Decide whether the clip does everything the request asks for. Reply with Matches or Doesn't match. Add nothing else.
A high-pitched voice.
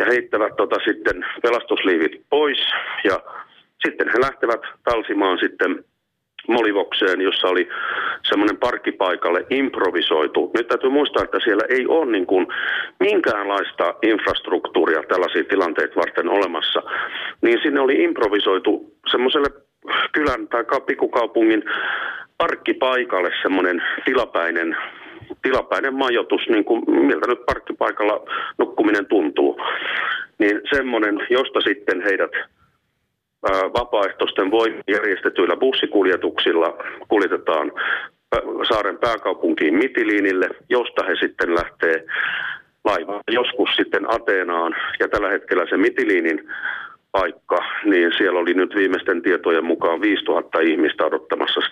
Matches